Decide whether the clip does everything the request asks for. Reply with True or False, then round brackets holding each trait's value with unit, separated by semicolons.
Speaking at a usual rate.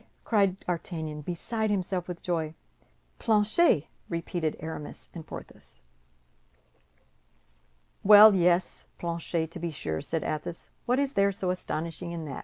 False (125 wpm)